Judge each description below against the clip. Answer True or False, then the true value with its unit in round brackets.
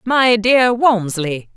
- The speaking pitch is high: True (220 Hz)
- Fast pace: False (115 wpm)